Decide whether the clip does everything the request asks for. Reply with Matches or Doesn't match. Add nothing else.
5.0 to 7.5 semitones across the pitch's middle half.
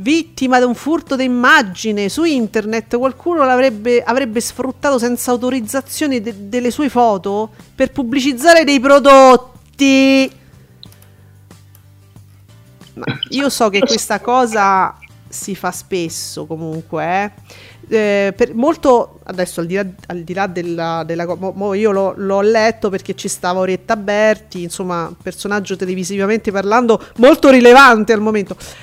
Matches